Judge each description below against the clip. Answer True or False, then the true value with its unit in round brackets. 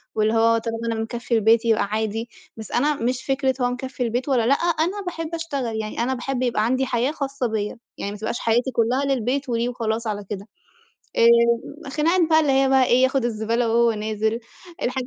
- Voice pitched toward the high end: True (240 Hz)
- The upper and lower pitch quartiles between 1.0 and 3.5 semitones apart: True (3.1 semitones)